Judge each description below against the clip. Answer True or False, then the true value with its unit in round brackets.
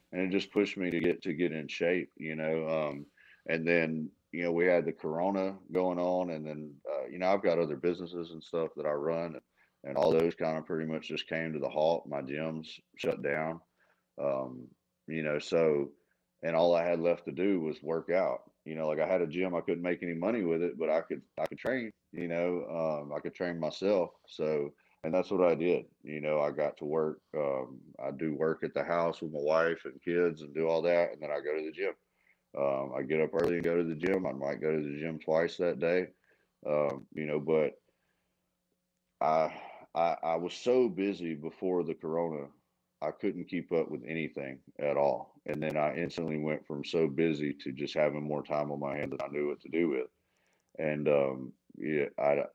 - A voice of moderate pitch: False (80 Hz)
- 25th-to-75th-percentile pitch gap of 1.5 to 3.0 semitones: True (2.4 semitones)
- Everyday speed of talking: False (225 wpm)